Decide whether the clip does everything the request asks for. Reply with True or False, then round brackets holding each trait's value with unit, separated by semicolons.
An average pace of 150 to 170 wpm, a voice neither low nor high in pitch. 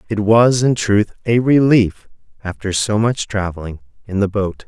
False (165 wpm; 105 Hz)